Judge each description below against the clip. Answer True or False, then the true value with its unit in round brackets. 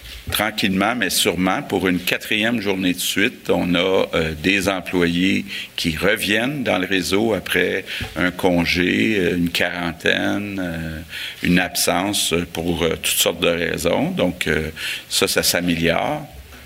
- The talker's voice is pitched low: True (90 Hz)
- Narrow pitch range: True (2.2 semitones)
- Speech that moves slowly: True (135 wpm)